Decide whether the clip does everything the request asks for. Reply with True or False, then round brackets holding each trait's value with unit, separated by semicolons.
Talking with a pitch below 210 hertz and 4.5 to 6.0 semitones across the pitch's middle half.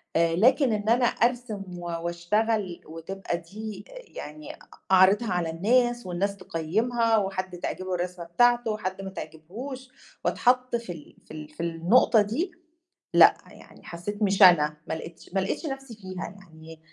True (195 Hz; 5.1 semitones)